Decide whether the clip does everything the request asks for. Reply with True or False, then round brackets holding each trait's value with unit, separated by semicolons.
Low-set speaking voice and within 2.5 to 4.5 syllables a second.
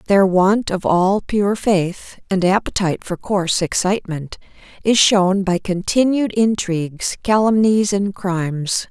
False (195 Hz; 4.0 syllables/s)